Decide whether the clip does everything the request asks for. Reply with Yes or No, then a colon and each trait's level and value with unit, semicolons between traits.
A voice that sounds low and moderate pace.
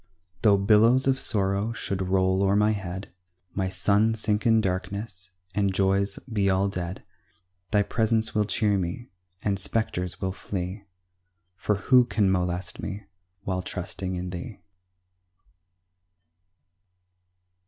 No: low, 100 Hz; slow, 125 wpm